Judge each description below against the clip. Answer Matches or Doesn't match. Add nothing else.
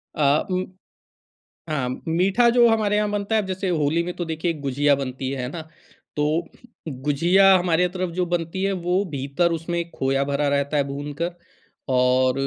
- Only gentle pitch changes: Doesn't match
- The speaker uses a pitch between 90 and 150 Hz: Doesn't match